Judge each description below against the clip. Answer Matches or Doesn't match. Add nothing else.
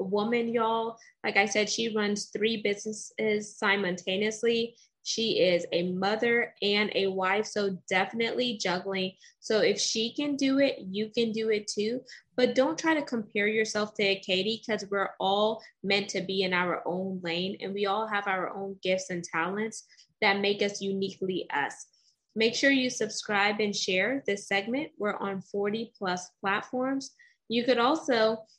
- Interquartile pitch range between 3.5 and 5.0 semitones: Doesn't match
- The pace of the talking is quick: Doesn't match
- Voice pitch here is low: Doesn't match